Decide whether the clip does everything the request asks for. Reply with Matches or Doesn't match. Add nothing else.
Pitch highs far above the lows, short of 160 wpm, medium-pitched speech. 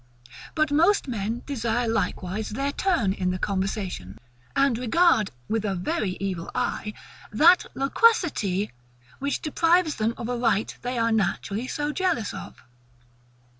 Doesn't match